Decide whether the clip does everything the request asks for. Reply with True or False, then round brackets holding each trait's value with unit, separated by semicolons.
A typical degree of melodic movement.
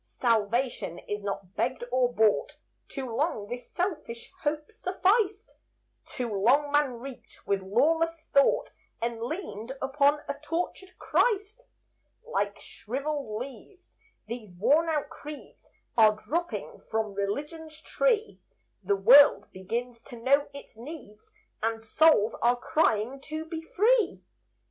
False (6.2 semitones)